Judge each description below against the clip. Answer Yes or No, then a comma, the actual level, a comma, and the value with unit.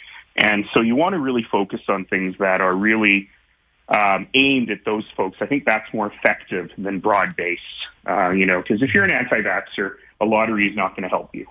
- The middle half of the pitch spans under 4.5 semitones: Yes, narrow, 2.5 semitones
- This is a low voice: Yes, low, 105 Hz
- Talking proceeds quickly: Yes, fast, 210 wpm